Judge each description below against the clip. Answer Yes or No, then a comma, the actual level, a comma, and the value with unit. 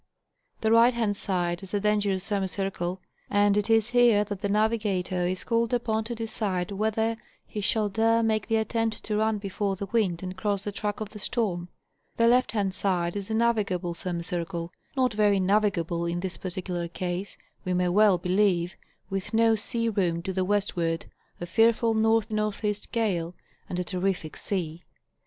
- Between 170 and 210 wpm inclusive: Yes, average, 175 wpm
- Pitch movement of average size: Yes, average, 3.4 semitones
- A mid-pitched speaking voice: No, high, 205 Hz